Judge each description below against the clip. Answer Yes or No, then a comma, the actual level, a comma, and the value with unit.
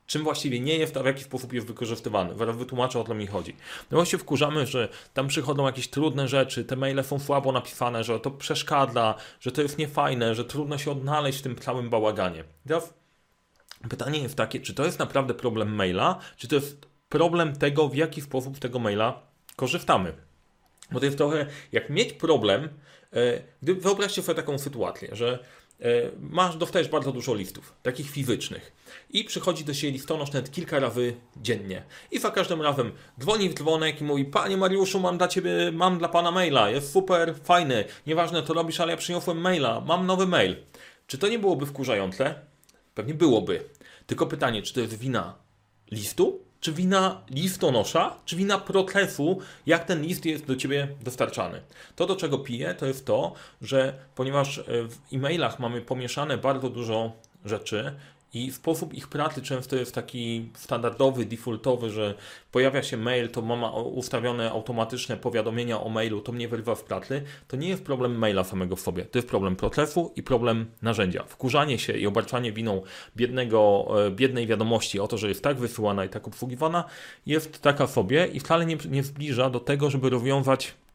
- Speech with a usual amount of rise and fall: Yes, average, 4.9 semitones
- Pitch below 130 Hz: No, low, 135 Hz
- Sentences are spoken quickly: Yes, fast, 175 wpm